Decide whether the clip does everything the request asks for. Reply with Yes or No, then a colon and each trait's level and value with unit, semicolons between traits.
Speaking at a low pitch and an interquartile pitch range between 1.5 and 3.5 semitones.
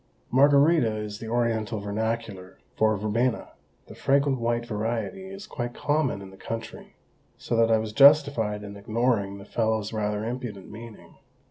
Yes: low, 115 Hz; average, 2.8 semitones